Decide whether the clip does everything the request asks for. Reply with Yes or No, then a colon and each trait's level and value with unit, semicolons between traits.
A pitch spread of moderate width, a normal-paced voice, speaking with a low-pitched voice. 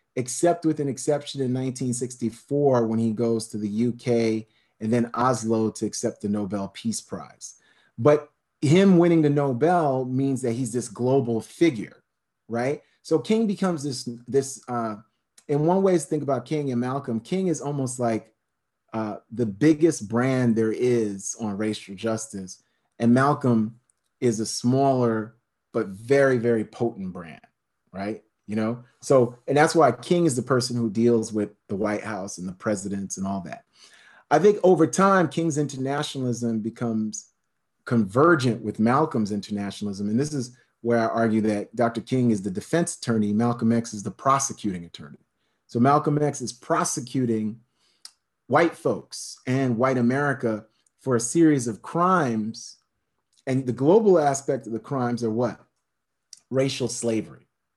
Yes: average, 4.1 semitones; average, 155 wpm; low, 120 Hz